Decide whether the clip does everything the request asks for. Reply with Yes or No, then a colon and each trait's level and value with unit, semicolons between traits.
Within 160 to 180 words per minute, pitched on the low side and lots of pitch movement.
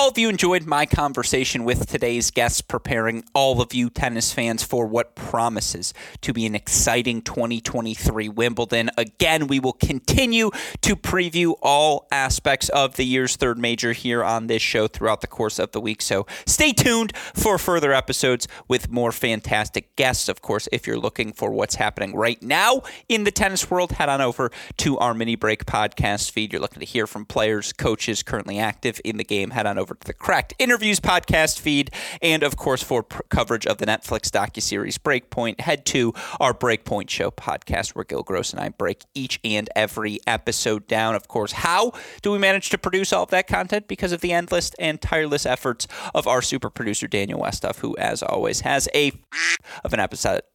No: average, 195 wpm; low, 125 Hz; wide, 5.9 semitones